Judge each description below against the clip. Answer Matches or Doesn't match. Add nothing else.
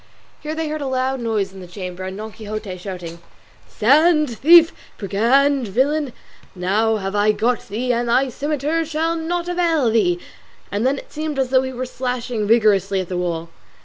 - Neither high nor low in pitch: Doesn't match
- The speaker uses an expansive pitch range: Matches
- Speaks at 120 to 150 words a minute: Doesn't match